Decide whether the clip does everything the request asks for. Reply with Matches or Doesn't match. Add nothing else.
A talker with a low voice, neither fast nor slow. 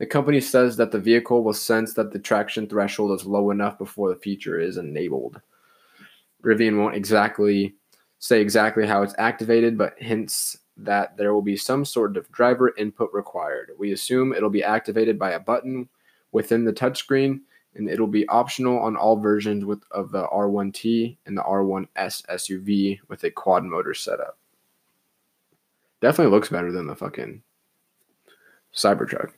Matches